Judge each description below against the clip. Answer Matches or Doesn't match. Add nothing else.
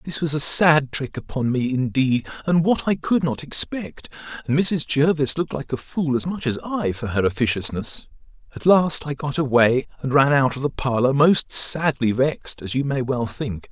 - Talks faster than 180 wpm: Matches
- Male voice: Matches